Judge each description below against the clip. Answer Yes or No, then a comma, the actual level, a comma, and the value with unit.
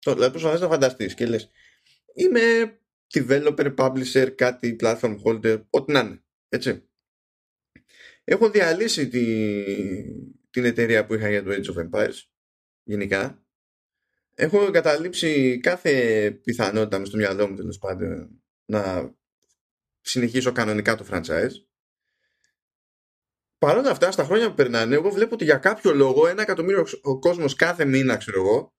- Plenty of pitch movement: Yes, wide, 8.1 semitones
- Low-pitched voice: Yes, low, 125 Hz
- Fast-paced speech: No, average, 135 wpm